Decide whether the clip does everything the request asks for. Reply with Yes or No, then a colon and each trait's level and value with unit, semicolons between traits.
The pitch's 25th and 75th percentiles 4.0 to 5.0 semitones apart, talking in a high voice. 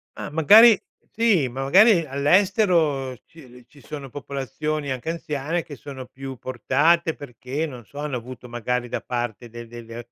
No: average, 4.5 semitones; medium, 140 Hz